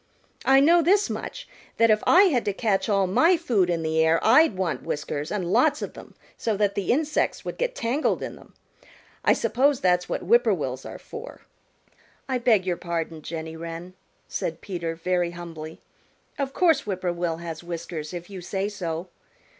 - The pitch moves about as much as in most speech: No, wide, 7.0 semitones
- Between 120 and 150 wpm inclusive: No, average, 190 wpm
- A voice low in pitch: No, high, 190 Hz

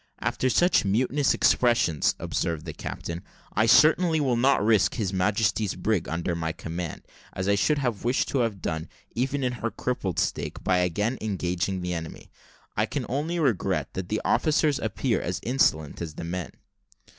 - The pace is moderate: Yes, average, 170 wpm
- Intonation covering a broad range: Yes, wide, 6.3 semitones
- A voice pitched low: Yes, low, 105 Hz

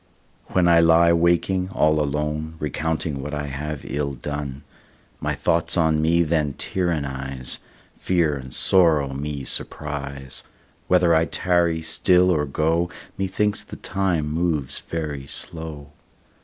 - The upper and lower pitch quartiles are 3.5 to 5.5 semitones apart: No, average, 2.8 semitones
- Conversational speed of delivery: No, slow, 130 wpm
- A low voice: Yes, very low, 80 Hz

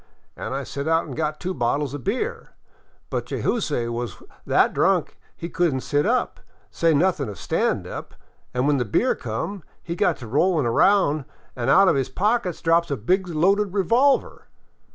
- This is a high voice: No, medium, 160 Hz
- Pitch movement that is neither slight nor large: No, wide, 5.9 semitones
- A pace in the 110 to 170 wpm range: No, average, 180 wpm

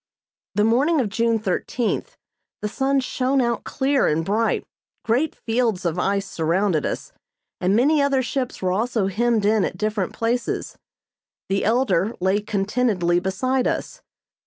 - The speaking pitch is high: Yes, high, 225 Hz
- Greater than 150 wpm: No, average, 145 wpm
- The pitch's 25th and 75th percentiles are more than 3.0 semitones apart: Yes, average, 4.5 semitones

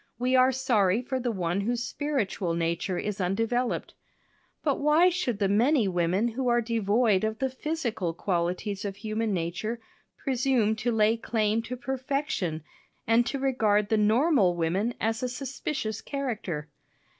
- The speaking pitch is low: No, high, 225 Hz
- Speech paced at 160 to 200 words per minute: No, average, 150 wpm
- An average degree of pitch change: Yes, average, 4.3 semitones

